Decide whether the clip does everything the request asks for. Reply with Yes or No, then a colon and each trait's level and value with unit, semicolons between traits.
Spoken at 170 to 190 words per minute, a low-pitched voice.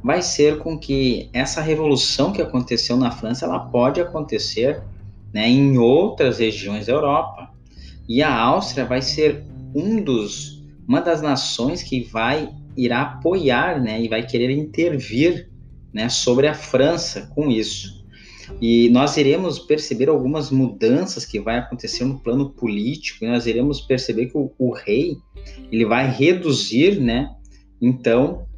No: average, 145 wpm; low, 125 Hz